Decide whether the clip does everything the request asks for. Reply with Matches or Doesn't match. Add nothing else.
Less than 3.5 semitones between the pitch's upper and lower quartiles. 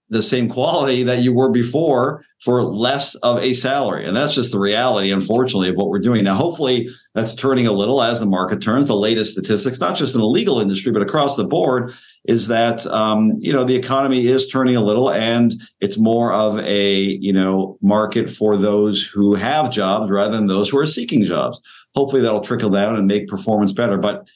Doesn't match